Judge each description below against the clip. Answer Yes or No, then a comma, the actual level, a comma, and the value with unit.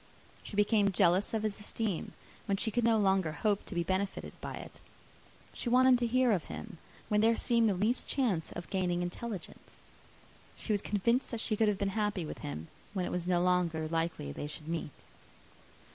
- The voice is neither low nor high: No, high, 200 Hz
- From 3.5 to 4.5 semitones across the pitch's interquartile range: Yes, average, 4.1 semitones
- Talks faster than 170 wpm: Yes, average, 195 wpm